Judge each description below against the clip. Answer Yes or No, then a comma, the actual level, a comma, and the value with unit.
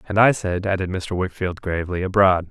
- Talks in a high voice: No, very low, 95 Hz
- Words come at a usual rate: Yes, average, 190 wpm